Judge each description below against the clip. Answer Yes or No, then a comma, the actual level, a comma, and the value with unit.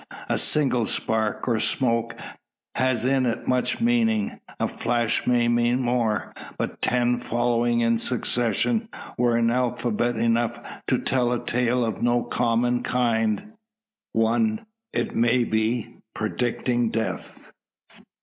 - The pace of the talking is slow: Yes, slow, 125 wpm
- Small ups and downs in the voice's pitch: Yes, narrow, 1.3 semitones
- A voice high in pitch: No, low, 120 Hz